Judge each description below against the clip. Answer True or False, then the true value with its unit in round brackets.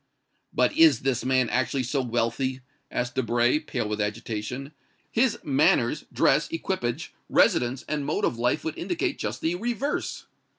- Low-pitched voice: True (130 Hz)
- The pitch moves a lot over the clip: True (5.8 semitones)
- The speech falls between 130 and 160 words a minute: True (145 wpm)